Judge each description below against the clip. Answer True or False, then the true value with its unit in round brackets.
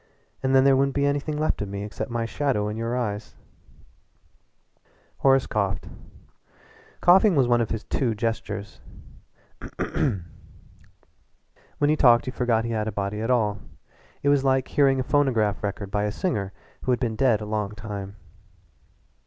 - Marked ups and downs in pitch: False (4.4 semitones)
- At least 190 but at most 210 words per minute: False (160 wpm)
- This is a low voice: True (115 Hz)